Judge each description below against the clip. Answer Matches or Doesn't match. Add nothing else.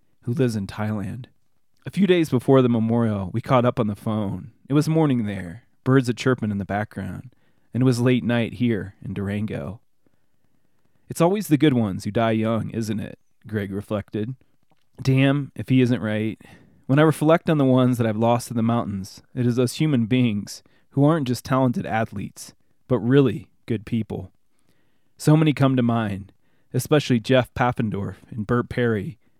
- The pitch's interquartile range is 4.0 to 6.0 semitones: Doesn't match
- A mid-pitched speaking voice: Doesn't match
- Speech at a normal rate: Matches